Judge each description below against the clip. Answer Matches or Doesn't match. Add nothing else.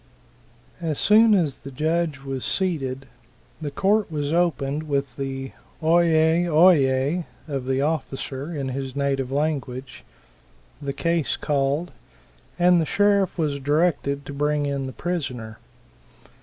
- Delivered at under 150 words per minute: Matches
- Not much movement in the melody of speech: Doesn't match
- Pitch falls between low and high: Matches